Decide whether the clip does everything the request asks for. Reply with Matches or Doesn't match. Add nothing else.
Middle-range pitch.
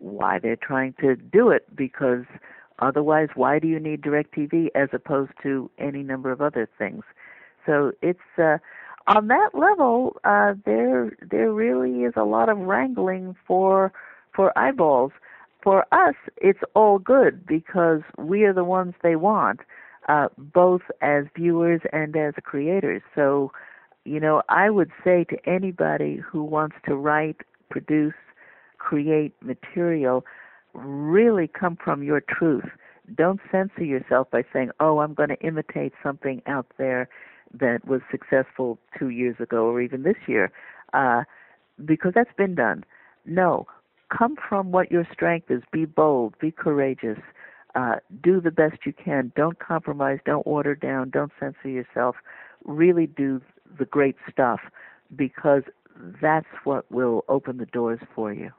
Matches